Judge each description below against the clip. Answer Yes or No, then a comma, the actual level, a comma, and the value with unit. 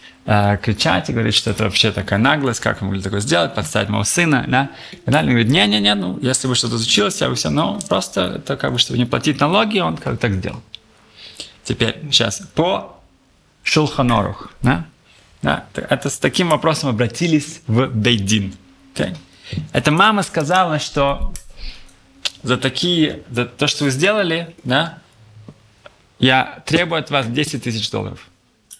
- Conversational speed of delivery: No, fast, 165 wpm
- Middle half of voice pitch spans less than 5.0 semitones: No, wide, 5.4 semitones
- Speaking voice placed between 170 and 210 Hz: No, low, 125 Hz